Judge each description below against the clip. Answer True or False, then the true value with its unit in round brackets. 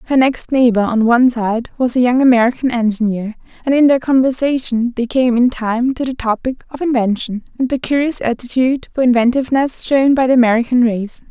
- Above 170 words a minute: True (185 wpm)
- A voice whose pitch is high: True (245 Hz)